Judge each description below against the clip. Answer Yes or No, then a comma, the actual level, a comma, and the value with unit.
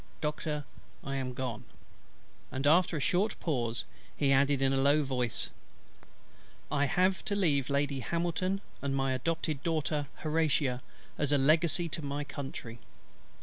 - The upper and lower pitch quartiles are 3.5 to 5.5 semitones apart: No, average, 3.1 semitones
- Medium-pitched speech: Yes, medium, 145 Hz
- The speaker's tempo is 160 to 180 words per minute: No, average, 145 wpm